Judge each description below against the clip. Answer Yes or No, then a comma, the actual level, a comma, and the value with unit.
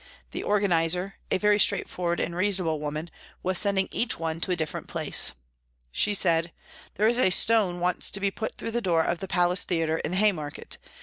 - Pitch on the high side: No, medium, 180 Hz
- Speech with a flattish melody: No, average, 3.4 semitones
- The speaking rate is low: No, average, 200 wpm